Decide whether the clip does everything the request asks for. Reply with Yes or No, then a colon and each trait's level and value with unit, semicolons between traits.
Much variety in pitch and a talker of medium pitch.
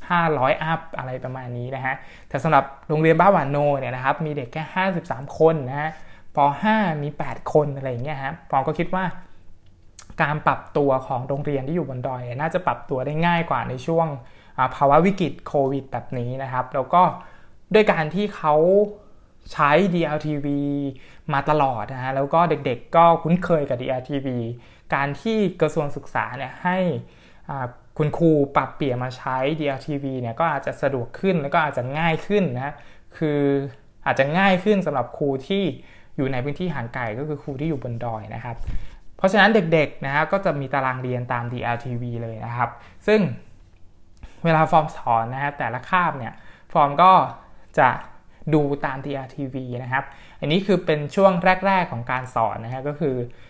No: average, 4.2 semitones; medium, 145 Hz